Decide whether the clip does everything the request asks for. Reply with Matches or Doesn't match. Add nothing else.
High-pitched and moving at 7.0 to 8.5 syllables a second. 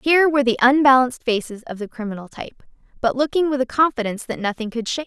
Matches